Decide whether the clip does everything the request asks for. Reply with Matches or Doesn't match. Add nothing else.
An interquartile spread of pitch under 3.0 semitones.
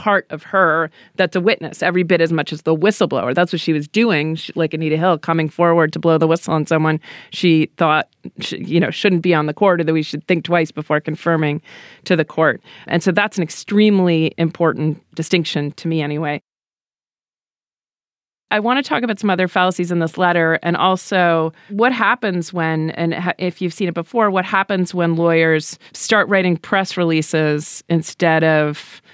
Matches